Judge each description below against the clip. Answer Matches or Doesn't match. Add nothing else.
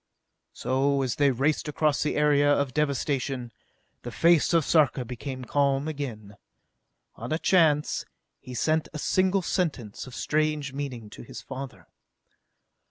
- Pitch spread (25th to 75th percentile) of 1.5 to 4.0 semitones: Matches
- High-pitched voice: Doesn't match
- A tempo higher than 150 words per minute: Doesn't match